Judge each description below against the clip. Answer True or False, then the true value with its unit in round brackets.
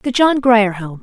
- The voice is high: True (230 Hz)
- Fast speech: True (235 wpm)